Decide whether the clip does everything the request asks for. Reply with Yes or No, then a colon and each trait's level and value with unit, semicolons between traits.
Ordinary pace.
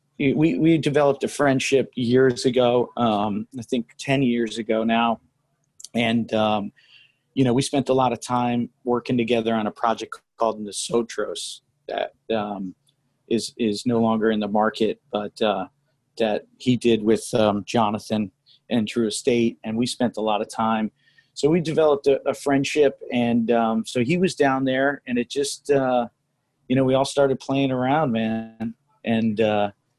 Yes: average, 170 wpm